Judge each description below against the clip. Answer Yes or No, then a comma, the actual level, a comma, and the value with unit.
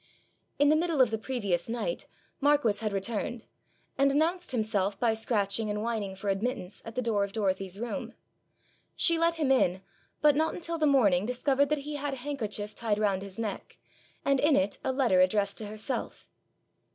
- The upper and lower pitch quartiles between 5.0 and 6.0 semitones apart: Yes, wide, 5.5 semitones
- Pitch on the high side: Yes, high, 230 Hz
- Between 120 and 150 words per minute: No, average, 185 wpm